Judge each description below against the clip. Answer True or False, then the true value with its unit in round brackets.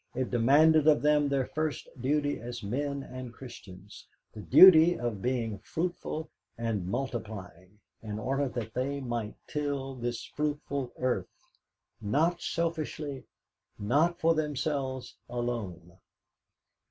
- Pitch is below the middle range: True (130 Hz)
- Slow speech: True (115 wpm)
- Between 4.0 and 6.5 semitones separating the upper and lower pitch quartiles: True (4.5 semitones)